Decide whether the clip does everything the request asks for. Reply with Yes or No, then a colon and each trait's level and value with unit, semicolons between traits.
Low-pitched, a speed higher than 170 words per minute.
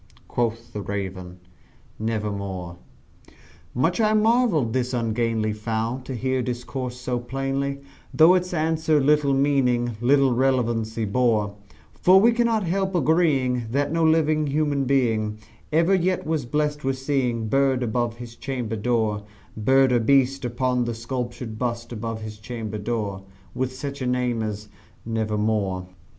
No: low, 125 Hz; slow, 135 wpm